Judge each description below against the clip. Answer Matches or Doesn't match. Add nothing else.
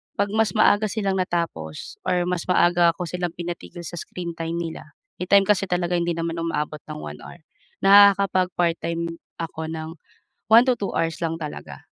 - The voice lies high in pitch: Doesn't match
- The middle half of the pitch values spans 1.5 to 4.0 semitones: Matches